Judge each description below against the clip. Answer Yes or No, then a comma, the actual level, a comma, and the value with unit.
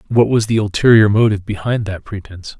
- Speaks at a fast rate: No, average, 185 wpm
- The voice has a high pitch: No, low, 105 Hz